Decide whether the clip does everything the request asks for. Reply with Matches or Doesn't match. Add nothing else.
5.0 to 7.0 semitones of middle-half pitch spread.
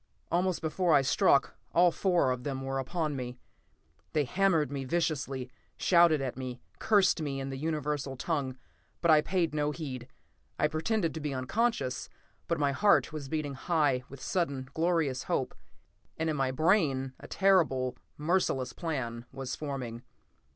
Doesn't match